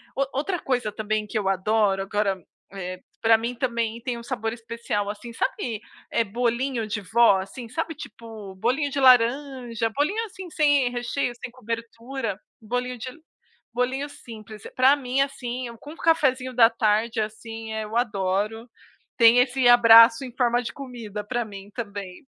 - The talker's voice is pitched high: Yes, high, 235 Hz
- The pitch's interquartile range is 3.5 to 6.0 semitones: No, average, 2.9 semitones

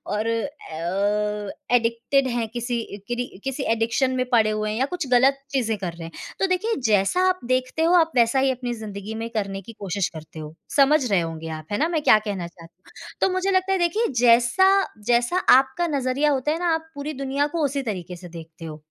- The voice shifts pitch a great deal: Yes, wide, 5.9 semitones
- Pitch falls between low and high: No, high, 240 Hz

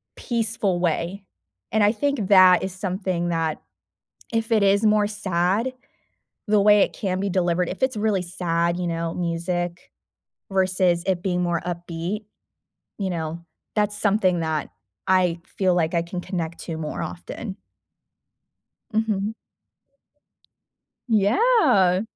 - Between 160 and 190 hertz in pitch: Yes, medium, 185 Hz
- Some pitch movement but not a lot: Yes, average, 3.2 semitones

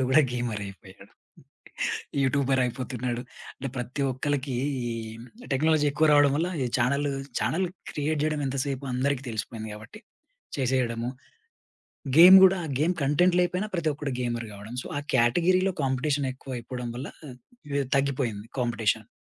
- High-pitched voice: No, low, 135 Hz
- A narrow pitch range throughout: No, average, 3.6 semitones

